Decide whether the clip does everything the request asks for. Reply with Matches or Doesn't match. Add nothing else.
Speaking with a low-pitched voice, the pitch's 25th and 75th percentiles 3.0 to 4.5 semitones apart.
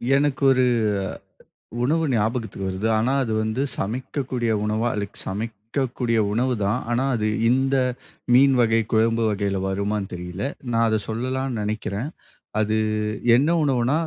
Matches